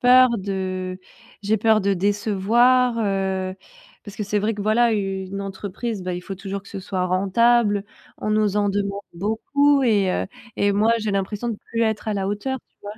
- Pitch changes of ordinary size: No, narrow, 2.3 semitones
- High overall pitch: Yes, high, 205 Hz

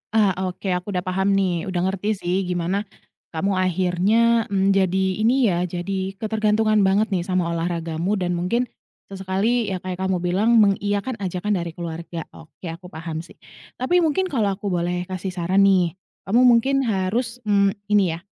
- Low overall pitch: No, high, 190 Hz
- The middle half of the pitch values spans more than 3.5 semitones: No, average, 2.9 semitones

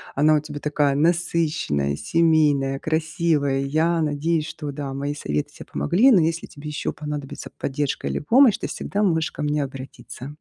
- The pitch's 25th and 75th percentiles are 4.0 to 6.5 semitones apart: No, narrow, 2.4 semitones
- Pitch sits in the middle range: Yes, medium, 150 Hz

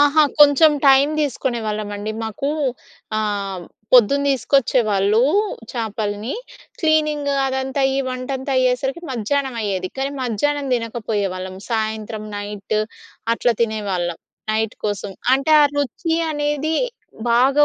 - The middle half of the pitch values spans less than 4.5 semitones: No, average, 4.8 semitones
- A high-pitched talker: Yes, high, 240 Hz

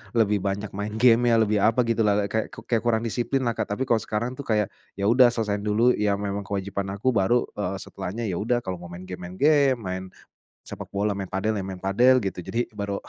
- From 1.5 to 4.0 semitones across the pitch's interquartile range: Yes, average, 3.2 semitones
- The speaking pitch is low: Yes, low, 105 Hz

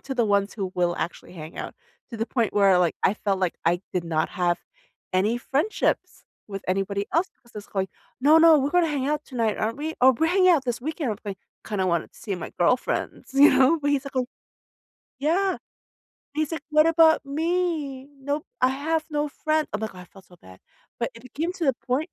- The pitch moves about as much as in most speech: No, wide, 7.5 semitones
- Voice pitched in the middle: No, very high, 260 Hz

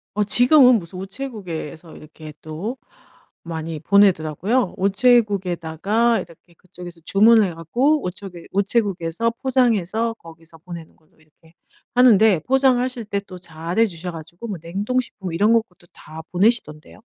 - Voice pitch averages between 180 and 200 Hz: Yes, high, 190 Hz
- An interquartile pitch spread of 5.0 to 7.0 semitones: Yes, wide, 5.6 semitones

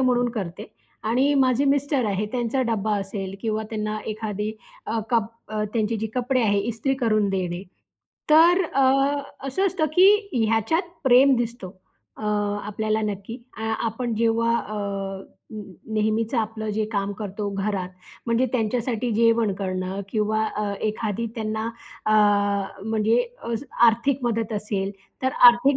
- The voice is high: Yes, high, 225 Hz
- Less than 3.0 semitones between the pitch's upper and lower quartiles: Yes, narrow, 2.5 semitones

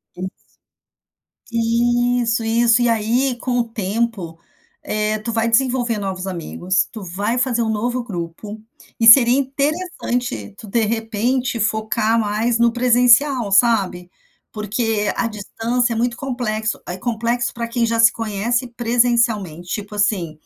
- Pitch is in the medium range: No, high, 230 Hz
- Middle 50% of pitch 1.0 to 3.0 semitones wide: Yes, narrow, 2.4 semitones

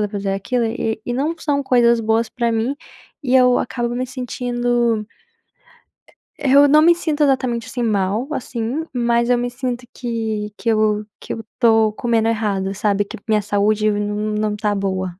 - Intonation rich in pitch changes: No, average, 2.8 semitones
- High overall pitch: Yes, high, 230 Hz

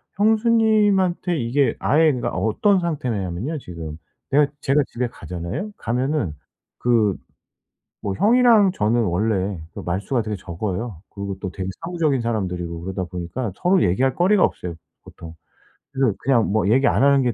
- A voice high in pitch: No, low, 120 Hz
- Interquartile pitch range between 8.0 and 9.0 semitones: Yes, wide, 8.7 semitones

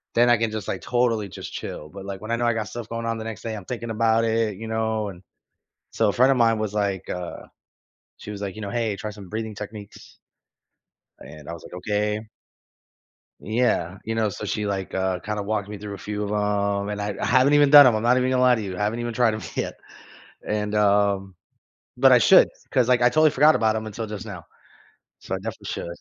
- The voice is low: Yes, low, 110 Hz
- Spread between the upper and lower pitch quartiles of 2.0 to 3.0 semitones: Yes, narrow, 2.4 semitones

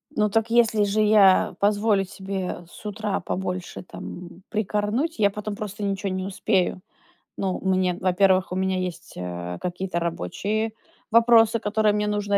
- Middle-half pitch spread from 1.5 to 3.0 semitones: Yes, narrow, 2.4 semitones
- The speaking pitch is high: Yes, high, 200 Hz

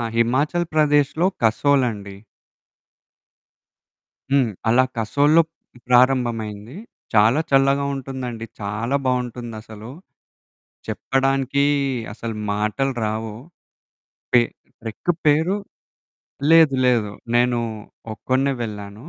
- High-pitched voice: No, low, 125 Hz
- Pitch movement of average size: Yes, average, 3.8 semitones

